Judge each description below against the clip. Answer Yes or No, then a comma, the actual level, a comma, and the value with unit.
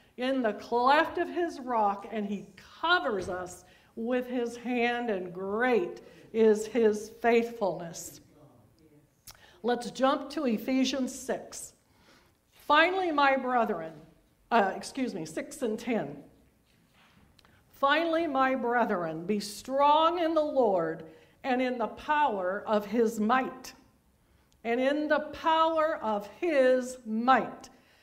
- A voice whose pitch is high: Yes, high, 240 Hz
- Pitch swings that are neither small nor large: Yes, average, 4.6 semitones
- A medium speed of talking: No, slow, 115 wpm